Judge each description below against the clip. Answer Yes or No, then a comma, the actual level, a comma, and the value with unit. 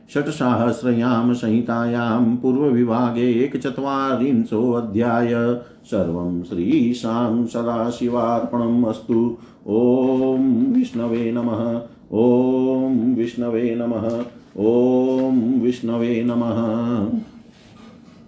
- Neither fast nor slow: No, slow, 65 wpm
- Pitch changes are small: Yes, narrow, 1.6 semitones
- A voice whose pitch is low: Yes, low, 120 Hz